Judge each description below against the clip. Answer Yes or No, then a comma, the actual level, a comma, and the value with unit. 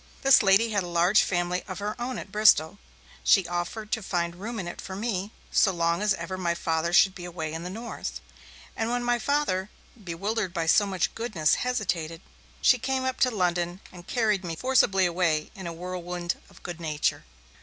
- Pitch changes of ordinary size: Yes, average, 3.9 semitones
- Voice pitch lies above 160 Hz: Yes, medium, 185 Hz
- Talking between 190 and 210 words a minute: Yes, average, 195 wpm